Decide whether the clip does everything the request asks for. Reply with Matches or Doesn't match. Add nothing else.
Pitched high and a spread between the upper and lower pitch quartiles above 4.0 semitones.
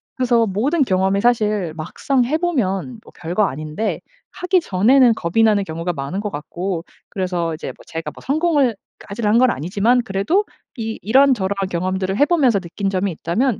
Matches